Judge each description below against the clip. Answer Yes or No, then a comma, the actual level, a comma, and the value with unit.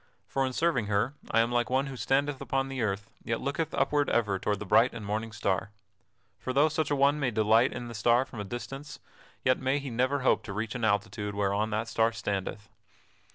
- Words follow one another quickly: Yes, fast, 220 wpm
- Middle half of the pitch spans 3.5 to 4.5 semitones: Yes, average, 4.2 semitones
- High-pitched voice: No, low, 120 Hz